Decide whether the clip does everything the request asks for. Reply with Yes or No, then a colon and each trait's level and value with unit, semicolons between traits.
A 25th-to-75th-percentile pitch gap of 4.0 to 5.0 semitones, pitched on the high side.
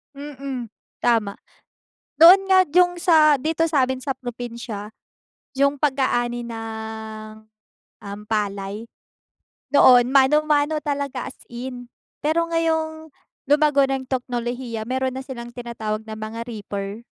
Yes: average, 4.5 semitones; very high, 255 Hz